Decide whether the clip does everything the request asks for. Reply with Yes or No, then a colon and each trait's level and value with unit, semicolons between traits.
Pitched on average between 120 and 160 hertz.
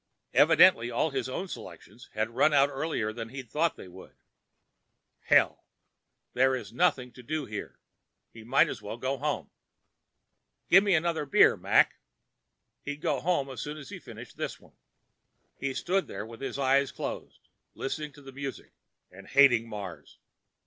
Yes: low, 135 Hz